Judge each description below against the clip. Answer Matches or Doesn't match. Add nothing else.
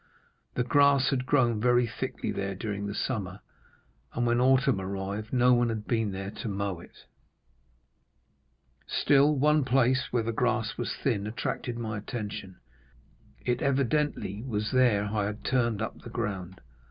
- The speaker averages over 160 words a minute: Doesn't match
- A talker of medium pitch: Doesn't match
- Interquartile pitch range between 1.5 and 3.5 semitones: Doesn't match